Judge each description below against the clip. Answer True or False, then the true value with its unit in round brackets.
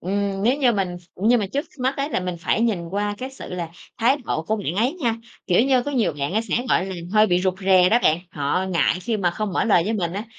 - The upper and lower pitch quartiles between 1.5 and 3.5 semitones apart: False (4.4 semitones)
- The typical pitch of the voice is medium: False (200 Hz)